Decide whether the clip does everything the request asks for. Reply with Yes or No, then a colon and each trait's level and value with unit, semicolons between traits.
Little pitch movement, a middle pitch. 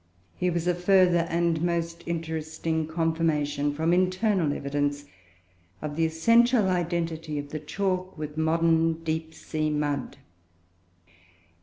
Yes: narrow, 2.1 semitones; medium, 165 Hz